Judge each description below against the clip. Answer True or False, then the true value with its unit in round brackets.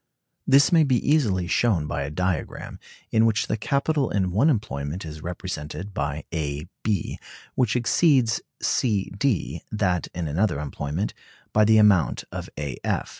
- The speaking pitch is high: False (95 Hz)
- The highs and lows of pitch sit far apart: True (6.8 semitones)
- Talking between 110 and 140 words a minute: False (165 wpm)